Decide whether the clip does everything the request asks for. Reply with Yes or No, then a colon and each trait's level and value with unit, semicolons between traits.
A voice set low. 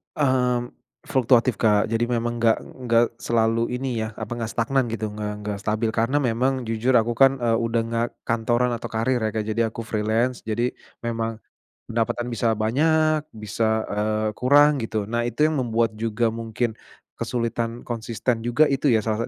Yes: low, 115 Hz